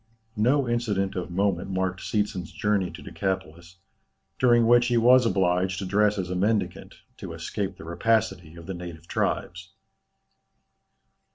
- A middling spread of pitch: Yes, average, 3.3 semitones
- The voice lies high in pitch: No, very low, 95 Hz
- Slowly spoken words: No, average, 145 wpm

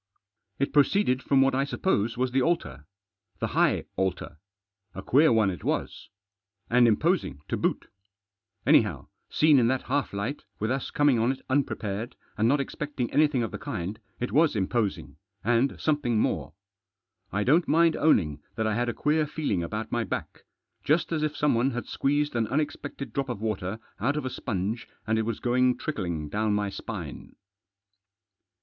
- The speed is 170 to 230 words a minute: Yes, average, 175 wpm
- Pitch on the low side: Yes, low, 120 Hz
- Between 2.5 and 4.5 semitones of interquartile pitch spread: No, average, 5.1 semitones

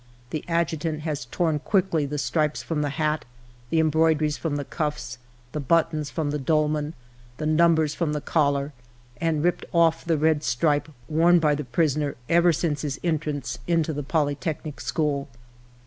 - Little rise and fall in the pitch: Yes, narrow, 1.9 semitones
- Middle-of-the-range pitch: Yes, medium, 155 Hz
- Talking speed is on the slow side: No, average, 170 wpm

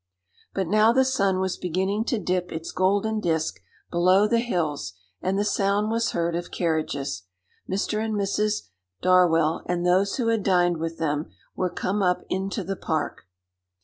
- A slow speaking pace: No, average, 165 wpm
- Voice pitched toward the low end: No, medium, 185 Hz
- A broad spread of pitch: No, average, 3.5 semitones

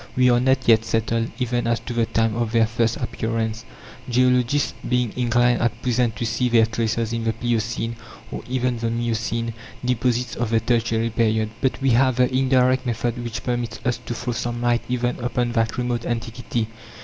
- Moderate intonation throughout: No, narrow, 1.4 semitones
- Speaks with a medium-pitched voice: No, low, 120 Hz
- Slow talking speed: No, average, 185 wpm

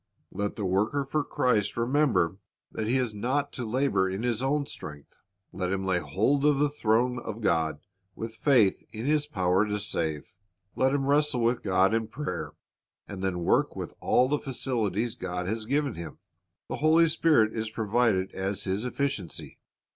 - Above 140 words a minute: Yes, average, 175 wpm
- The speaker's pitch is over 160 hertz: No, low, 110 Hz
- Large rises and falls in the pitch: Yes, wide, 6.0 semitones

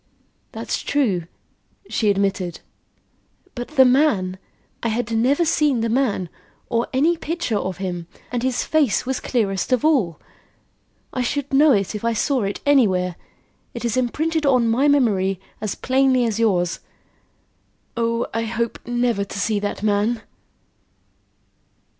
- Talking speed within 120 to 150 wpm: Yes, average, 140 wpm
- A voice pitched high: Yes, high, 235 Hz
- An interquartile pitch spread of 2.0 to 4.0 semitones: No, average, 4.7 semitones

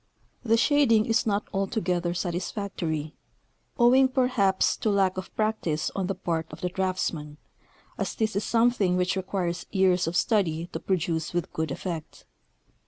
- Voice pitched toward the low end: No, high, 190 Hz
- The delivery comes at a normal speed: Yes, average, 155 wpm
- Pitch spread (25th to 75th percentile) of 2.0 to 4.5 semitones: Yes, average, 4.0 semitones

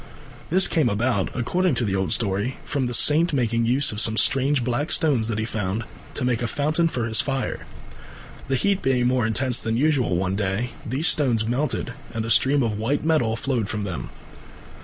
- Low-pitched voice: Yes, low, 120 Hz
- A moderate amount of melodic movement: Yes, average, 4.1 semitones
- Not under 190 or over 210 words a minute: Yes, average, 200 wpm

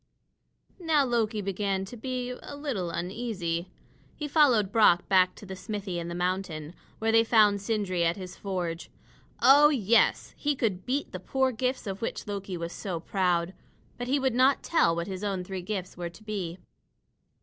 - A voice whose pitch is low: No, high, 200 Hz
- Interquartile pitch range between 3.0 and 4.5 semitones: No, average, 5.1 semitones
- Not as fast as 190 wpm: Yes, average, 180 wpm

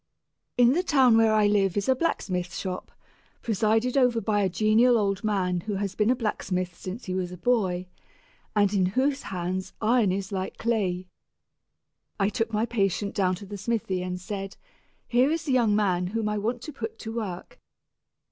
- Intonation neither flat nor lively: Yes, average, 3.8 semitones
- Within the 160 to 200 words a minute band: Yes, average, 185 wpm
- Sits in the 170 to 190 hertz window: No, high, 210 Hz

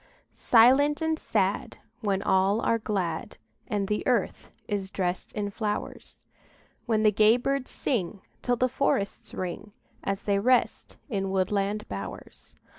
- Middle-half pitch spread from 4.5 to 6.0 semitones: No, average, 3.5 semitones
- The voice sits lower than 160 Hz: No, high, 210 Hz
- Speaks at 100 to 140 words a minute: Yes, slow, 135 wpm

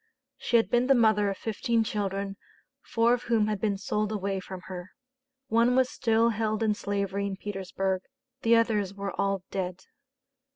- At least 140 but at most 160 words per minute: No, average, 170 wpm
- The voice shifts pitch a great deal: No, narrow, 2.6 semitones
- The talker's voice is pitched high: Yes, high, 210 Hz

